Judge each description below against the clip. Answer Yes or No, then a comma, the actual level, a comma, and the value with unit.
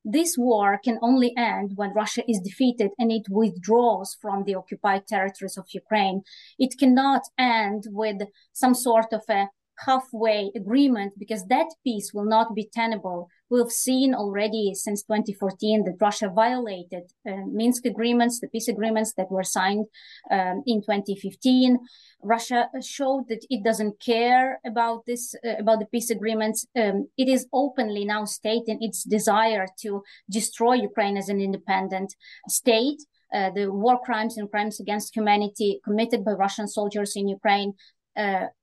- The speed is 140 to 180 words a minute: Yes, average, 150 wpm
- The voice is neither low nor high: No, high, 220 Hz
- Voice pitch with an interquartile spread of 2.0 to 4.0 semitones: Yes, average, 2.9 semitones